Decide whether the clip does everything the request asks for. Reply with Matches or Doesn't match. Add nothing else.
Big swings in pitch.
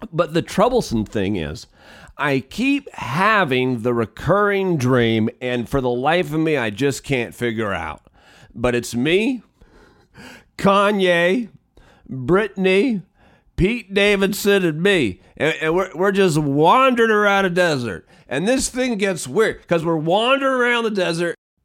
Matches